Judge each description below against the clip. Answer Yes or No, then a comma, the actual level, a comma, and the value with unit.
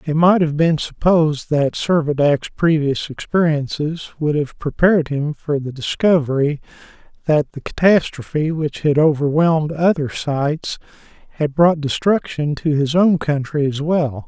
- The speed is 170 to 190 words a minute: No, average, 140 wpm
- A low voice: No, medium, 150 Hz